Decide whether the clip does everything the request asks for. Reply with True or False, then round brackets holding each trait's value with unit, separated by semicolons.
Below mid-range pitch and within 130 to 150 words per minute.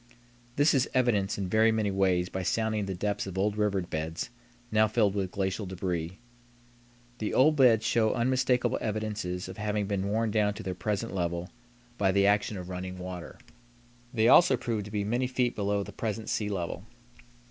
False (105 Hz; 180 wpm)